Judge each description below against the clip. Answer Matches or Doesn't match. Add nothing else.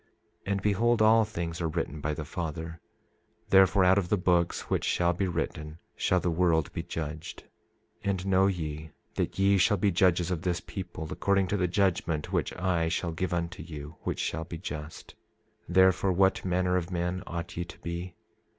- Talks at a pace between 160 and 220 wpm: Matches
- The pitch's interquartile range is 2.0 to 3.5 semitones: Matches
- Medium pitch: Doesn't match